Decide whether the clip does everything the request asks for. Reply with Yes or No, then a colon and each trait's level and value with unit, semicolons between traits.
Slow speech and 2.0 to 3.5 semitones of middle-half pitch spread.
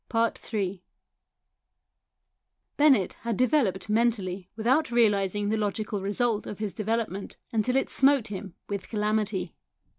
Yes: slow, 115 wpm; average, 2.8 semitones